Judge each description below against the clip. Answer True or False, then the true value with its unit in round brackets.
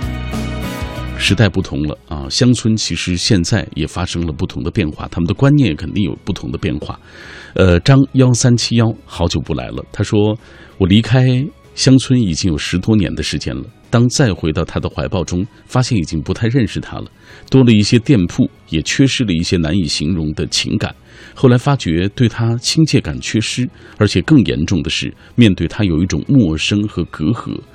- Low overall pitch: True (105 Hz)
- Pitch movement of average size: False (6.1 semitones)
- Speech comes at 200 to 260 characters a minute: False (280 characters per minute)